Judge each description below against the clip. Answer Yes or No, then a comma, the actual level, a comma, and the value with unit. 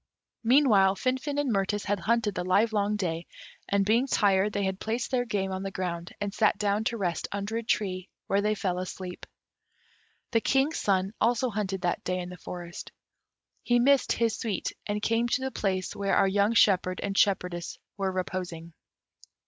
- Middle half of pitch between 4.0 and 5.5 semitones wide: No, average, 3.4 semitones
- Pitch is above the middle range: Yes, high, 200 Hz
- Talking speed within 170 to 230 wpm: Yes, average, 180 wpm